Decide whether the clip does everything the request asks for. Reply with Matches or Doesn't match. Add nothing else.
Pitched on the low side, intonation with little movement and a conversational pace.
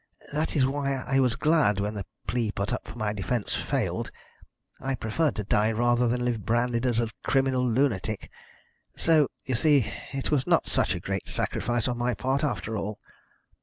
Doesn't match